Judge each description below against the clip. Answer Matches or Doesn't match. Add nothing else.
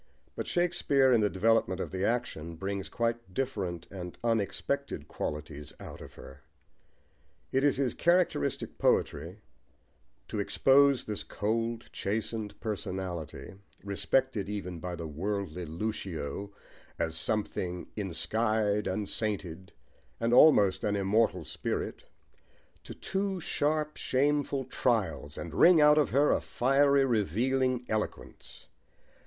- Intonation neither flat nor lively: Doesn't match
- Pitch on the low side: Matches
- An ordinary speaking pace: Doesn't match